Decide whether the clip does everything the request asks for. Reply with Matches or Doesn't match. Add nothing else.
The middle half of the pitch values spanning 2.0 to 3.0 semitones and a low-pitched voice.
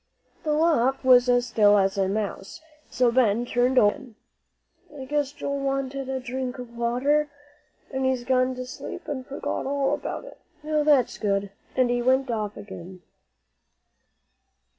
Doesn't match